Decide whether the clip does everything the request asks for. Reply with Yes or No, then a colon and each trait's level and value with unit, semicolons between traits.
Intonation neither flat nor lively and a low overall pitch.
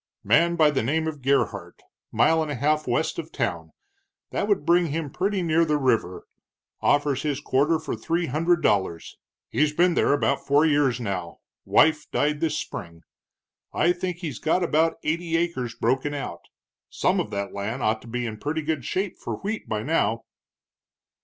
No: average, 4.7 semitones; medium, 150 Hz